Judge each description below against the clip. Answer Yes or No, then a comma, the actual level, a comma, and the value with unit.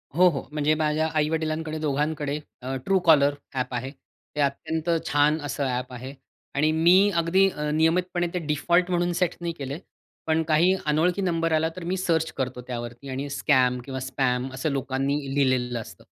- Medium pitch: Yes, medium, 150 Hz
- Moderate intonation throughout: Yes, average, 3.7 semitones